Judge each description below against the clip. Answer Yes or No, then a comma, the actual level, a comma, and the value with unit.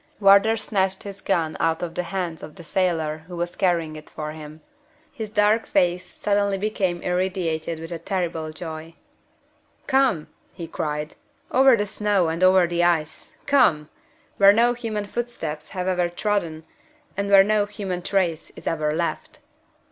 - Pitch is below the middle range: No, medium, 180 Hz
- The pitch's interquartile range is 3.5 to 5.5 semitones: Yes, average, 3.8 semitones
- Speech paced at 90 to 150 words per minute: No, average, 160 wpm